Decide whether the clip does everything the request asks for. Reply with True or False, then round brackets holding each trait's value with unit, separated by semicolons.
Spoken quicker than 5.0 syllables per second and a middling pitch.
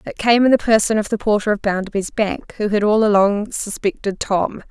False (5.3 syllables/s; 210 Hz)